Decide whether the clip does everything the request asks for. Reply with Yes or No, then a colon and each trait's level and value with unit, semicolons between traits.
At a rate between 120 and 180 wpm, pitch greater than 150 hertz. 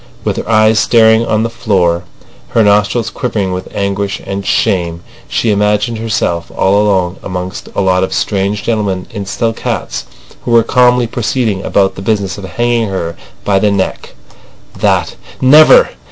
No: average, 155 wpm; low, 100 Hz